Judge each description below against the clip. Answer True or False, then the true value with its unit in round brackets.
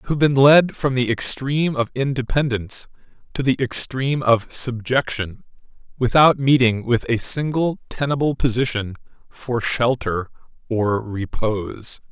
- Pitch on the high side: False (125 Hz)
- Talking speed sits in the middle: False (125 wpm)